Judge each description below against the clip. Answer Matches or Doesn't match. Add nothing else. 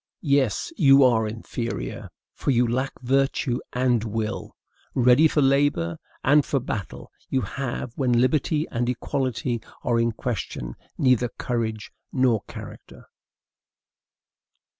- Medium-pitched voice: Doesn't match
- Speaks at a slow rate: Matches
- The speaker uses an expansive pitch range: Doesn't match